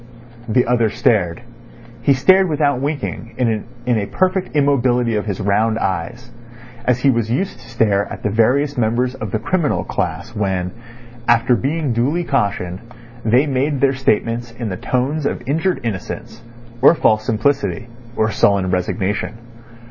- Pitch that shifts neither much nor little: Yes, average, 4.3 semitones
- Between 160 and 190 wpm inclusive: No, average, 150 wpm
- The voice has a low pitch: Yes, low, 120 Hz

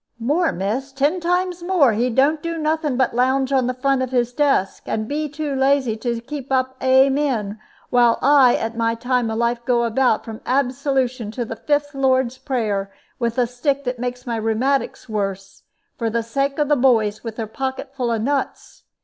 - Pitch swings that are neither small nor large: Yes, average, 3.1 semitones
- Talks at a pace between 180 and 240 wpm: Yes, average, 190 wpm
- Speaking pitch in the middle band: No, very high, 255 Hz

